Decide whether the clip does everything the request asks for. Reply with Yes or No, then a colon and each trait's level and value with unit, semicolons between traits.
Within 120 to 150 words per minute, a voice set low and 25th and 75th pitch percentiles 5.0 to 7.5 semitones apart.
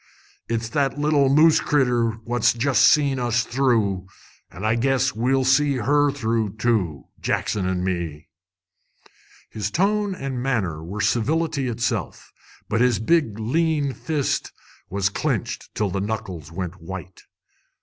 Yes: slow, 135 wpm; low, 120 Hz; wide, 5.6 semitones